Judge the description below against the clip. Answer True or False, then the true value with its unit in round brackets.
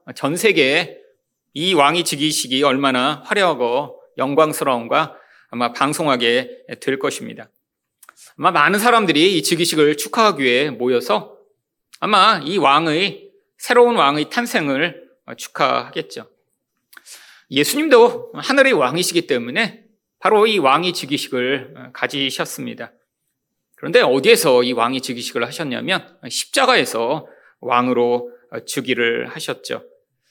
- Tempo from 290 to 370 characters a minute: False (270 characters per minute)